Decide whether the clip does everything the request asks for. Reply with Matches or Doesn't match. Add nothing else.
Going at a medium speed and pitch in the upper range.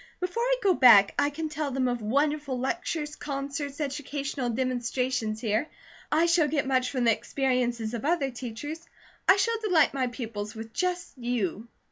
Matches